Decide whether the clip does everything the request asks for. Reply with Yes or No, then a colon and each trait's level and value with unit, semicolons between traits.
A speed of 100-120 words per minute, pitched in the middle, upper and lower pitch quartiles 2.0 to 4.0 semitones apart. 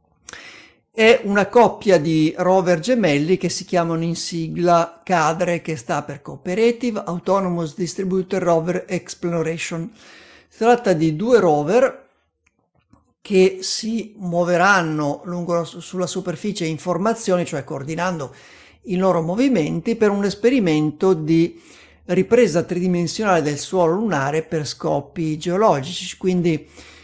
Yes: slow, 115 wpm; medium, 180 Hz; average, 2.8 semitones